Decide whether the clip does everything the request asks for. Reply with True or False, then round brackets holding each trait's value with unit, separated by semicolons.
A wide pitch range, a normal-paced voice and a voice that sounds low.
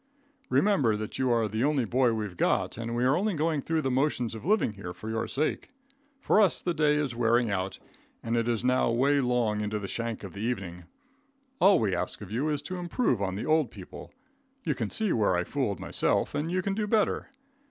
False (6.0 semitones; 225 wpm; 120 Hz)